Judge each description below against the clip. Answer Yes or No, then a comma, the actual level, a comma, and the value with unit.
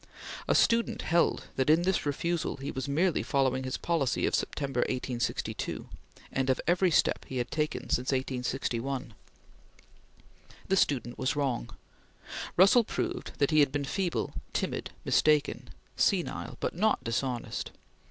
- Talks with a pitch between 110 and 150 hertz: Yes, medium, 140 Hz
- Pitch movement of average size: Yes, average, 4.7 semitones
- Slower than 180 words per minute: Yes, average, 140 wpm